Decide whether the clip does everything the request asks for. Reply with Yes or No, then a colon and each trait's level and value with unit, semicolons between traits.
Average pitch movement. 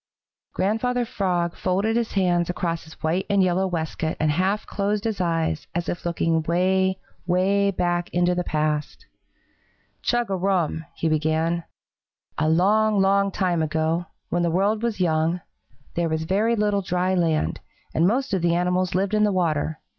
Yes: average, 3.1 semitones